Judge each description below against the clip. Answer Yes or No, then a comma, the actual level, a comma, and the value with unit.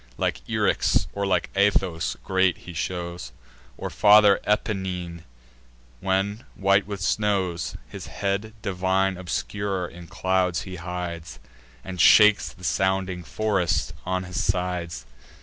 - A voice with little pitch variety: Yes, narrow, 1.8 semitones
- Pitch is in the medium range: No, very low, 95 Hz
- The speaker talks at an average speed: No, slow, 120 wpm